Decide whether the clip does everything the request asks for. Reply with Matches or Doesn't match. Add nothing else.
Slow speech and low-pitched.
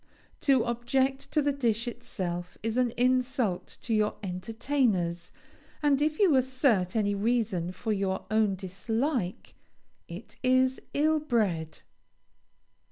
Doesn't match